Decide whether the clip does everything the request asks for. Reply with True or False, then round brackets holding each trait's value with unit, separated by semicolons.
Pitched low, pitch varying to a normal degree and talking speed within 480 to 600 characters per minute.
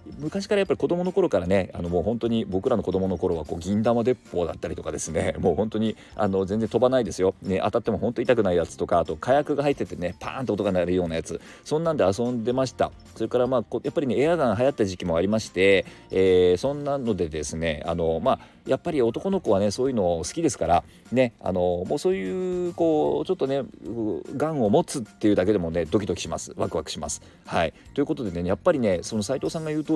False (110 Hz; 6.2 semitones; 485 characters per minute)